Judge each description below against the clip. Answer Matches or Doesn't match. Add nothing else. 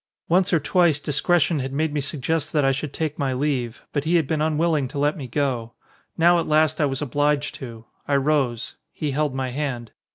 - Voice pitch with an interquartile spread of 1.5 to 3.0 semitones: Matches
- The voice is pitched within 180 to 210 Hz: Doesn't match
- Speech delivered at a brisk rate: Matches